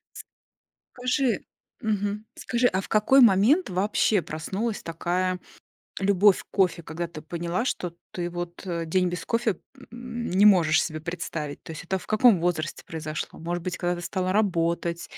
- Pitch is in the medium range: Yes, medium, 180 Hz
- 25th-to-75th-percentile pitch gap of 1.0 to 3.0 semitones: No, average, 3.7 semitones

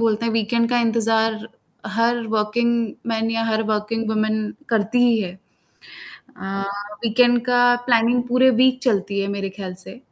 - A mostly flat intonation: Yes, narrow, 1.9 semitones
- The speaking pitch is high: Yes, high, 225 Hz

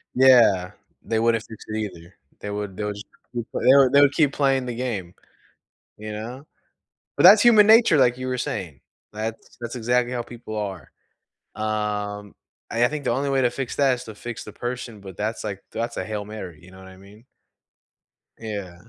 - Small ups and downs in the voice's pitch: No, average, 3.6 semitones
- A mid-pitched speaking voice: No, low, 115 Hz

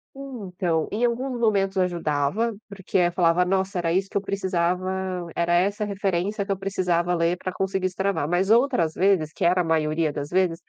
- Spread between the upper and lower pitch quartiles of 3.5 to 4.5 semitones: No, narrow, 2.6 semitones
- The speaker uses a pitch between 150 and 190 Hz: Yes, medium, 185 Hz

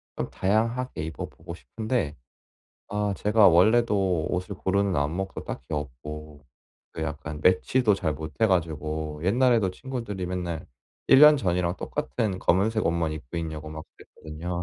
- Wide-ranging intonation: No, average, 5.0 semitones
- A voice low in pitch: Yes, very low, 90 Hz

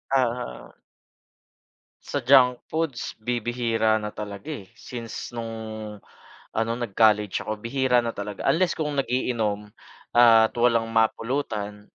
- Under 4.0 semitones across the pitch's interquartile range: Yes, average, 2.7 semitones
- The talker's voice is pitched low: Yes, low, 115 Hz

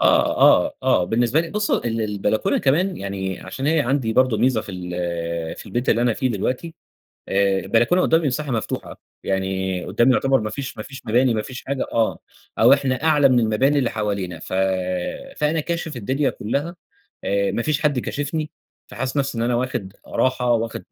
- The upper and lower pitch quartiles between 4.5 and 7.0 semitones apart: Yes, average, 4.8 semitones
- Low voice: Yes, low, 125 Hz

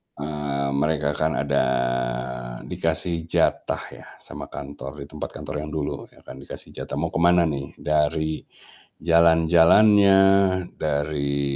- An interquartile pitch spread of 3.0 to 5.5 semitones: No, narrow, 2.6 semitones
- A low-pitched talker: Yes, very low, 75 Hz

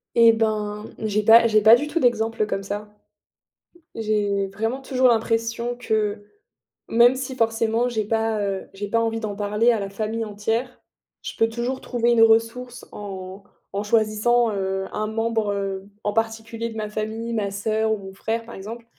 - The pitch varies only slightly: Yes, narrow, 1.8 semitones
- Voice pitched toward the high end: Yes, high, 220 Hz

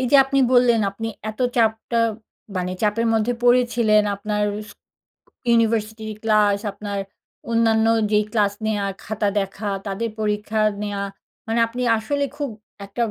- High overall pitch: Yes, high, 220 Hz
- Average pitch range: No, narrow, 1.9 semitones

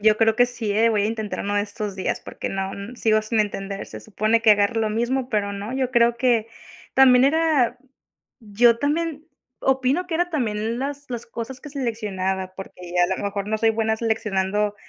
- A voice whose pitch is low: No, high, 225 Hz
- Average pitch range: Yes, average, 3.5 semitones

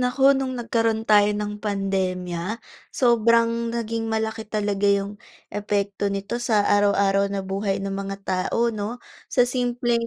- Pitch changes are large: No, average, 2.7 semitones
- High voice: Yes, high, 210 Hz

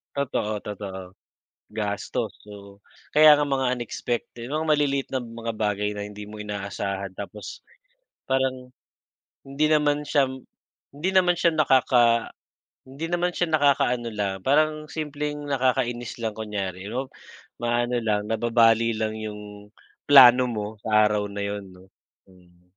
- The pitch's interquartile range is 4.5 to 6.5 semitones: Yes, average, 5.1 semitones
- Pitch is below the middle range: Yes, low, 115 Hz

